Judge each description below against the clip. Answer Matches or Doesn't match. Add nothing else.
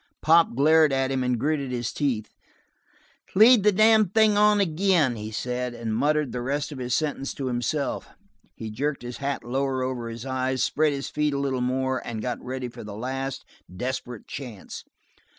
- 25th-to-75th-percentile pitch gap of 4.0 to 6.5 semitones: Doesn't match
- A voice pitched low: Matches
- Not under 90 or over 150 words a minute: Doesn't match